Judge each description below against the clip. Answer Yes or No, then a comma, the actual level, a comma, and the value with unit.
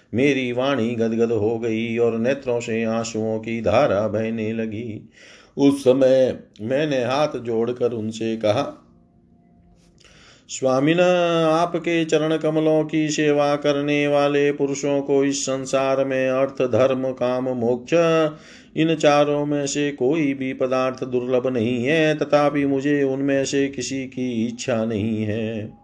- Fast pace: No, average, 130 wpm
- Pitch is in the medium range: No, low, 130 Hz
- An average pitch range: Yes, average, 4.0 semitones